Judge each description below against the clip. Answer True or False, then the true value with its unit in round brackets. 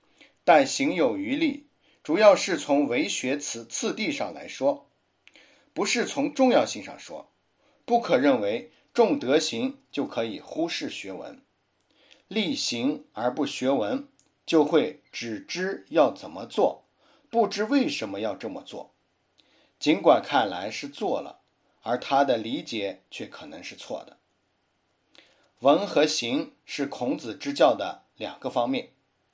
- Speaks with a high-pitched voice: True (265 Hz)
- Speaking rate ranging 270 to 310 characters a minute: False (190 characters per minute)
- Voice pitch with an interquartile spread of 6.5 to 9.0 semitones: True (7.1 semitones)